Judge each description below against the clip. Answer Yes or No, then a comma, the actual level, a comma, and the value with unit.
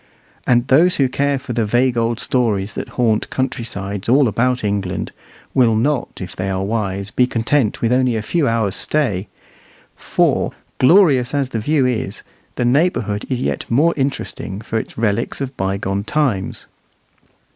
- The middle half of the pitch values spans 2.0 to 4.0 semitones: No, average, 4.4 semitones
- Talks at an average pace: Yes, average, 165 wpm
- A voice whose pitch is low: Yes, low, 120 Hz